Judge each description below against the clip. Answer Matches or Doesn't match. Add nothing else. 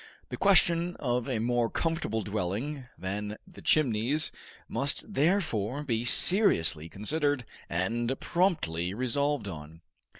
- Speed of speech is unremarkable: Doesn't match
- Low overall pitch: Matches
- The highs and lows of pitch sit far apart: Matches